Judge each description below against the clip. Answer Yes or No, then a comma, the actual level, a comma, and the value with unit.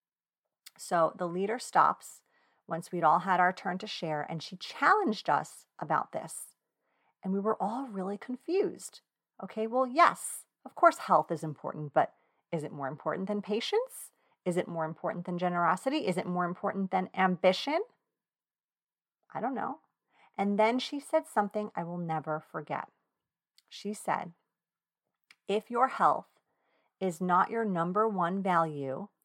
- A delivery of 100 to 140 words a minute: No, average, 150 wpm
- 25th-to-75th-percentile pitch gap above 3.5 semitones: Yes, average, 4.2 semitones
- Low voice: No, high, 190 Hz